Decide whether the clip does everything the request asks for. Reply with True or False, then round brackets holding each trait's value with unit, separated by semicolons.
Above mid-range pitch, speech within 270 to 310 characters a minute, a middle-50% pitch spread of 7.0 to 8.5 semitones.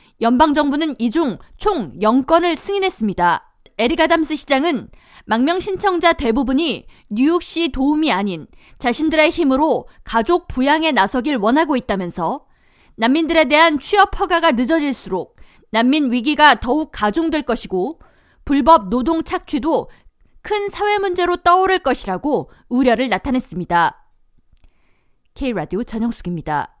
False (290 Hz; 295 characters per minute; 6.0 semitones)